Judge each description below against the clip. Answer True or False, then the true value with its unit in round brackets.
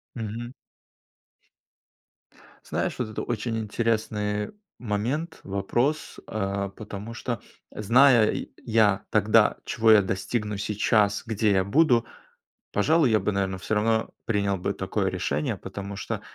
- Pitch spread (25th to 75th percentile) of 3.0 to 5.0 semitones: False (2.6 semitones)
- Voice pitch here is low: True (105 Hz)